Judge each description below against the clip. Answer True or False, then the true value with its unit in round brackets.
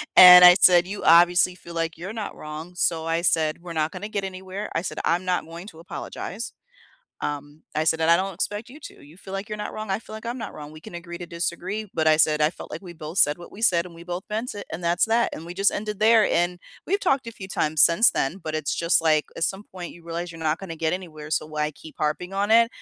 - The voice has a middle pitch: True (175 Hz)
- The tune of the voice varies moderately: True (3.5 semitones)